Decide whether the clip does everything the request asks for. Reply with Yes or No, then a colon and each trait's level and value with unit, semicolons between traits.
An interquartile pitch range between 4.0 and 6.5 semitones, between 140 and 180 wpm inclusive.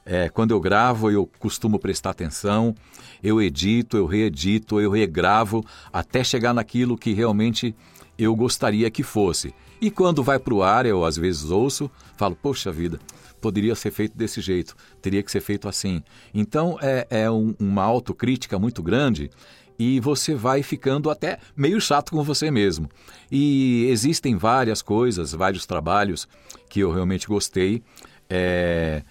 Yes: average, 4.7 semitones; average, 155 wpm